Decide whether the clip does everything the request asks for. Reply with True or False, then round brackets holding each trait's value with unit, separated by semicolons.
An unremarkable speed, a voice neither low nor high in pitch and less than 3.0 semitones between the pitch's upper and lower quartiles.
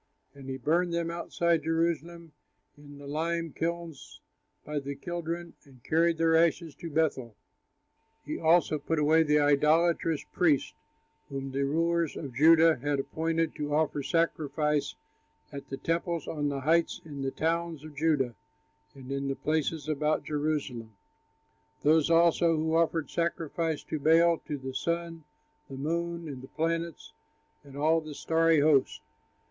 True (150 wpm; 155 Hz; 2.6 semitones)